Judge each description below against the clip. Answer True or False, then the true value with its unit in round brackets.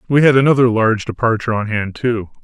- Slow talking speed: False (195 wpm)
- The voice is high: False (115 Hz)